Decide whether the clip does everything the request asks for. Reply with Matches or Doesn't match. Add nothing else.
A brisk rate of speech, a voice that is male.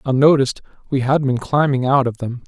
Doesn't match